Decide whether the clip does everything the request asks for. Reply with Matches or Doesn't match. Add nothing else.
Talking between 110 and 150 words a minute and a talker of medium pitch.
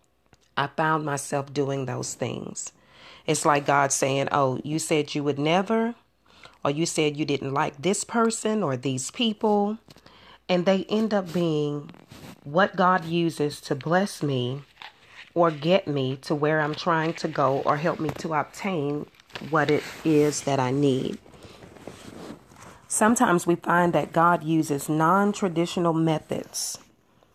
Matches